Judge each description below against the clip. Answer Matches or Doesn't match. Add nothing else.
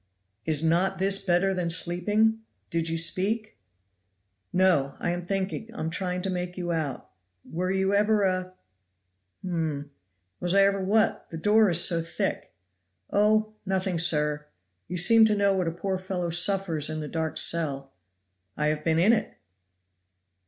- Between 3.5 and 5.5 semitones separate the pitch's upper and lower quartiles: Doesn't match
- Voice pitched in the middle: Matches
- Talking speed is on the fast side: Doesn't match